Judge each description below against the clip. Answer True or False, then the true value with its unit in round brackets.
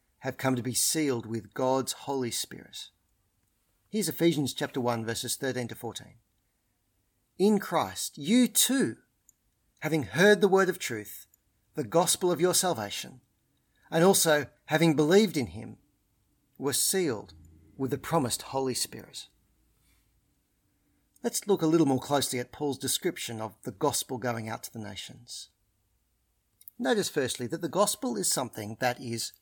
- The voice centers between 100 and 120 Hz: False (135 Hz)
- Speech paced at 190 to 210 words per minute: False (145 wpm)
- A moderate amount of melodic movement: False (6.0 semitones)